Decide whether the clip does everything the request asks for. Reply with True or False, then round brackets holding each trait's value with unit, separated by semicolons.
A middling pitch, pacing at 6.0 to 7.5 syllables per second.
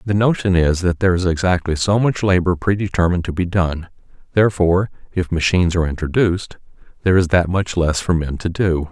False (90 Hz; 6.1 syllables/s)